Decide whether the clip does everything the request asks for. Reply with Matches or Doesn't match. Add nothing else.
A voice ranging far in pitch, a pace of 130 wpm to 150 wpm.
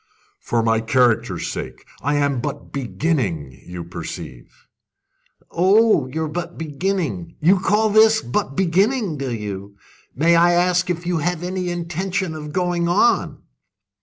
Matches